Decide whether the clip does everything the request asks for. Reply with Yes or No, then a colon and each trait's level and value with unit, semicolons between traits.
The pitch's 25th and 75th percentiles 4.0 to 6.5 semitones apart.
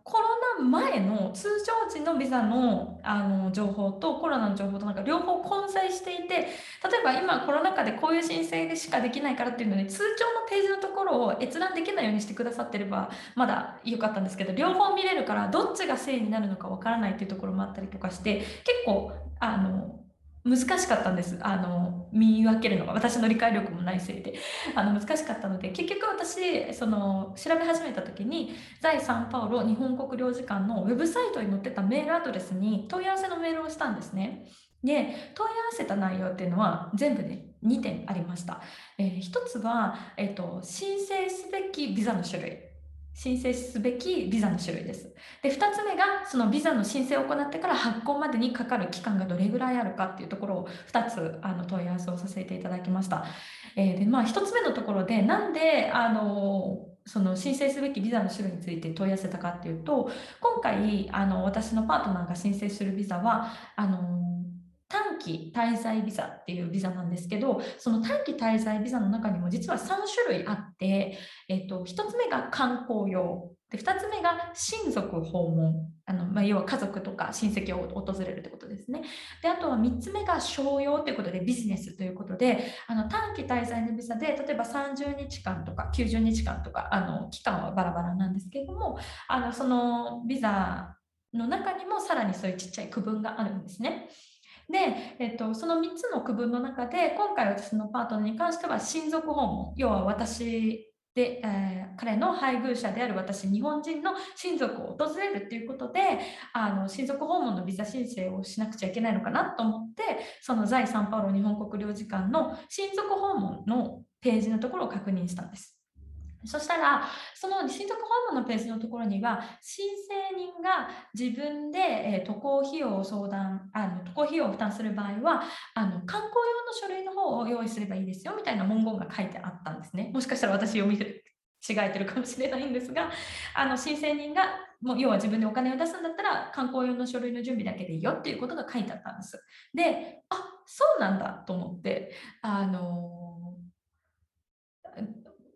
No: wide, 7.0 semitones